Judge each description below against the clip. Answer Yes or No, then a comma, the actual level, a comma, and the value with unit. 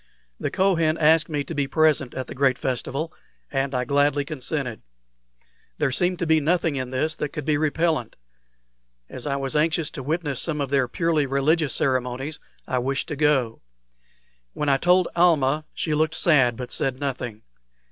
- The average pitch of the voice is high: No, medium, 145 Hz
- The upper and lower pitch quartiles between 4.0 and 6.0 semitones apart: No, average, 3.0 semitones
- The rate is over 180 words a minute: No, average, 175 wpm